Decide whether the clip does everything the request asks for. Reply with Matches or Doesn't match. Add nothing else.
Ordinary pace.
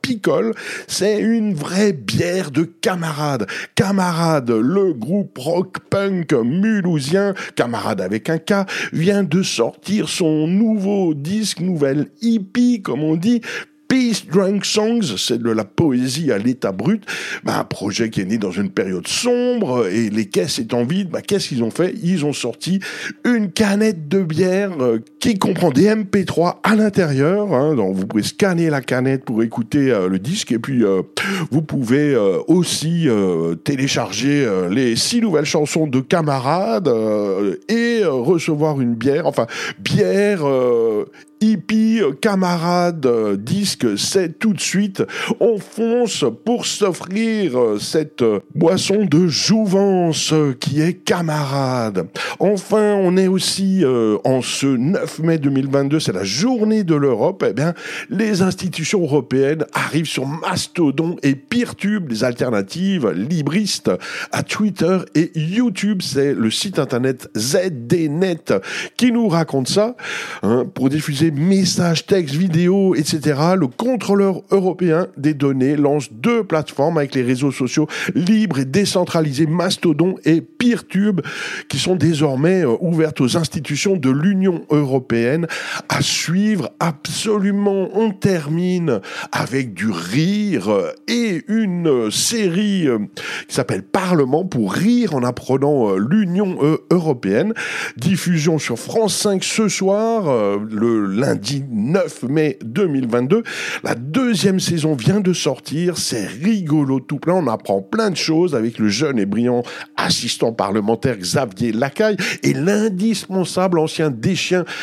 Doesn't match